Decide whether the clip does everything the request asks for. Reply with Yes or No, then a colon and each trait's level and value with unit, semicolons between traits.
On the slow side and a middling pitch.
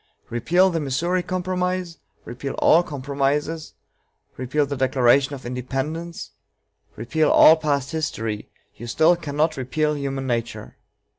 Yes: slow, 120 wpm; medium, 145 Hz